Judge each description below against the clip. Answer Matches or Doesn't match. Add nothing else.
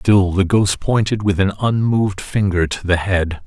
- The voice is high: Doesn't match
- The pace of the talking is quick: Doesn't match